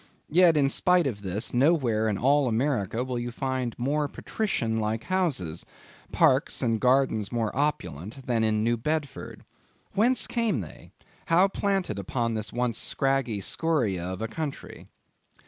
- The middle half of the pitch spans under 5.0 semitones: No, average, 5.3 semitones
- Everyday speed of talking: Yes, average, 145 wpm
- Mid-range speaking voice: No, low, 125 Hz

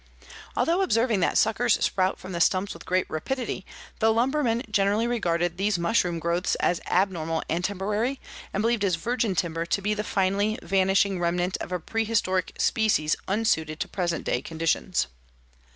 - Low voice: No, high, 195 Hz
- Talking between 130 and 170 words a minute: Yes, average, 160 wpm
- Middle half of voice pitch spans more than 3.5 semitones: Yes, average, 4.1 semitones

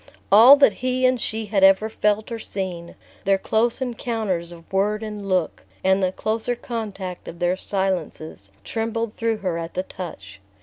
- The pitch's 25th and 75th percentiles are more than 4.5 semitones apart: No, average, 3.6 semitones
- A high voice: Yes, high, 200 Hz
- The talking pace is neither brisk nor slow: Yes, average, 170 wpm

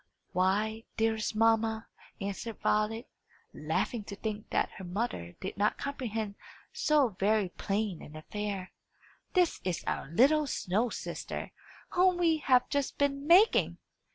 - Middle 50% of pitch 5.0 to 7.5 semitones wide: Yes, wide, 5.5 semitones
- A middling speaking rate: No, slow, 130 wpm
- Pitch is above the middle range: Yes, high, 220 Hz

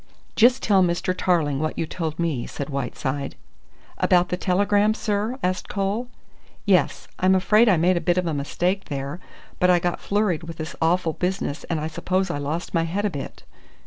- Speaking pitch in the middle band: Yes, medium, 175 Hz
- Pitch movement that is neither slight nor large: Yes, average, 3.5 semitones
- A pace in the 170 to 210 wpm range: Yes, average, 190 wpm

